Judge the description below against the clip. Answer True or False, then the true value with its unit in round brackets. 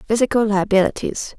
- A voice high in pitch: True (210 Hz)